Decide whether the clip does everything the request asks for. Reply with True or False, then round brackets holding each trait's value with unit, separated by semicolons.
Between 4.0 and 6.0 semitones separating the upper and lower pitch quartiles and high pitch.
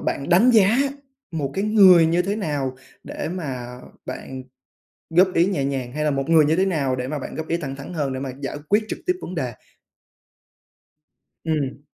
False (5.1 semitones; 155 Hz)